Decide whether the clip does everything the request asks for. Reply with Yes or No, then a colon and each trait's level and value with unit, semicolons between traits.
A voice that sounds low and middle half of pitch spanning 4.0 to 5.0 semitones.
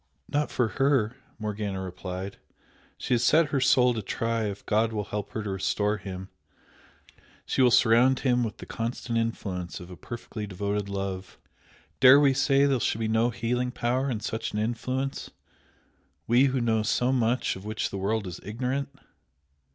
No: low, 115 Hz; average, 3.5 semitones